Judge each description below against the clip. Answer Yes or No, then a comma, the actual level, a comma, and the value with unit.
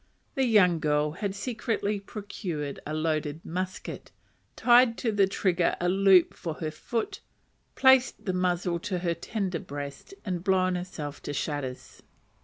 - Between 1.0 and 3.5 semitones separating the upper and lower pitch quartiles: No, average, 4.4 semitones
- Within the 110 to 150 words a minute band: Yes, average, 145 wpm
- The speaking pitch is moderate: Yes, medium, 180 Hz